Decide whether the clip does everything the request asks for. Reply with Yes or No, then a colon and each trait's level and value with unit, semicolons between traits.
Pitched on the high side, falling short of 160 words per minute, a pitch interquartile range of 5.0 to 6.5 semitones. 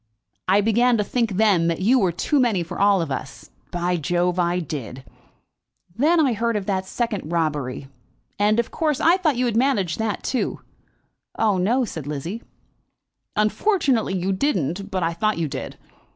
No: high, 200 Hz; average, 175 wpm; wide, 5.4 semitones